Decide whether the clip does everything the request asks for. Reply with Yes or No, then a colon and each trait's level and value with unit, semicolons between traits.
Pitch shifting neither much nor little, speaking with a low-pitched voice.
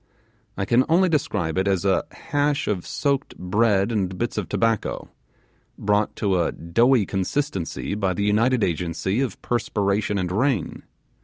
Yes: average, 4.5 semitones; low, 105 Hz